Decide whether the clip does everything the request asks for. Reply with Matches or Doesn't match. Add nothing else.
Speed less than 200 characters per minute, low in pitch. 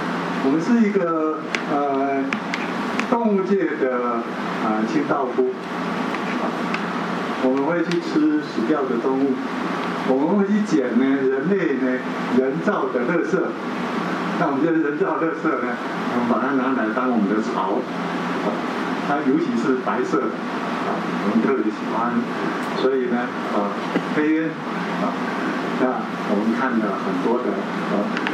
Doesn't match